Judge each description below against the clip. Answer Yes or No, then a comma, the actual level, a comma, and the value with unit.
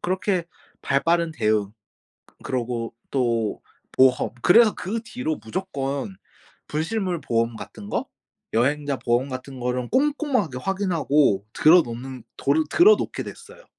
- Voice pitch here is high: No, medium, 140 Hz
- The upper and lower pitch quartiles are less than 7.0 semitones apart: No, wide, 7.5 semitones